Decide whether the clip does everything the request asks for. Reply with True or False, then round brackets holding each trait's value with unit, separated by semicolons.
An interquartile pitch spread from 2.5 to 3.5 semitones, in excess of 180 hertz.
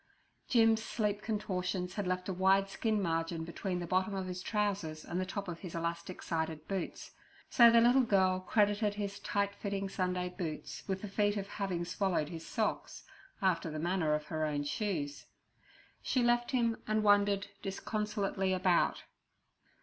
True (2.9 semitones; 190 Hz)